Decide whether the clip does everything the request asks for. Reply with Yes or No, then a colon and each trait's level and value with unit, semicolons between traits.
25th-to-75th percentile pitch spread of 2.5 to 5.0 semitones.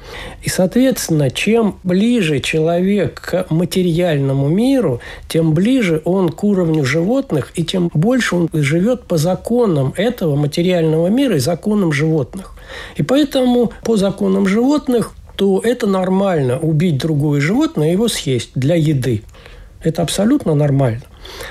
No: wide, 5.5 semitones